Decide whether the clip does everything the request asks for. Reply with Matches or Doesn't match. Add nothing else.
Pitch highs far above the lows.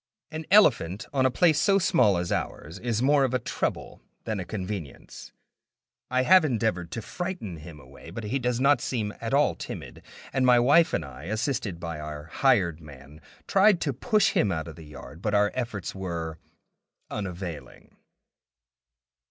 Matches